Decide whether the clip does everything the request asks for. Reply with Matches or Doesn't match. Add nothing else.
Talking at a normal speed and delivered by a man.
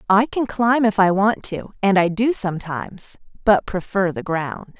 Doesn't match